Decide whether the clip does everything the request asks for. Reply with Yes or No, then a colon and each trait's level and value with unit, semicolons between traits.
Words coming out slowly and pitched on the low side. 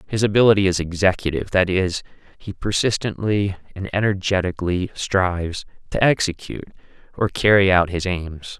Yes: slow, 125 wpm; very low, 95 Hz